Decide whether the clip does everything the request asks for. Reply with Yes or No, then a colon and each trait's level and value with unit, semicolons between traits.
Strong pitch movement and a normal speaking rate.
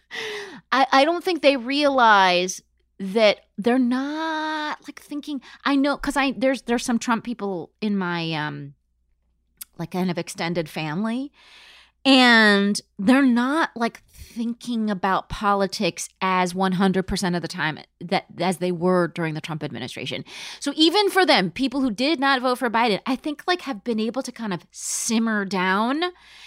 Yes: wide, 6.8 semitones; average, 160 wpm